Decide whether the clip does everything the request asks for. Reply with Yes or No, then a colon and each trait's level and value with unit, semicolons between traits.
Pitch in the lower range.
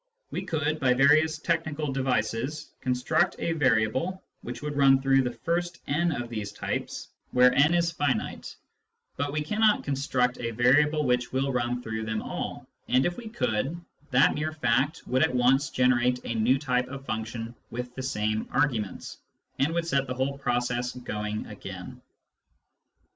Yes: low, 130 Hz